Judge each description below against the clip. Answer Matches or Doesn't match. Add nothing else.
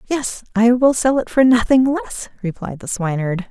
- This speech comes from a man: Doesn't match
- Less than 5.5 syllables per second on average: Matches